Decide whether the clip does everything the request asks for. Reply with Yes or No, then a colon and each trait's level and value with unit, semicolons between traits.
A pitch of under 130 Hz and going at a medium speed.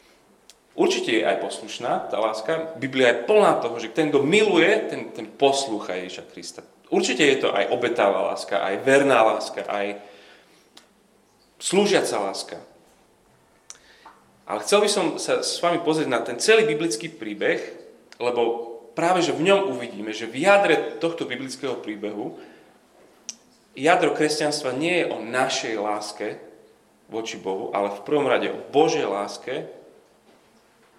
No: medium, 140 Hz; average, 140 wpm